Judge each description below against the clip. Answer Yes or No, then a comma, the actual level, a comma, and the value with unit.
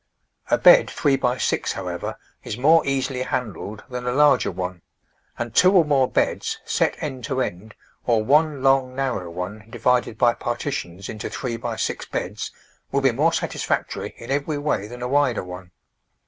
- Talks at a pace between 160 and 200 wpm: Yes, average, 175 wpm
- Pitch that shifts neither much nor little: Yes, average, 4.1 semitones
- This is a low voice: Yes, low, 125 Hz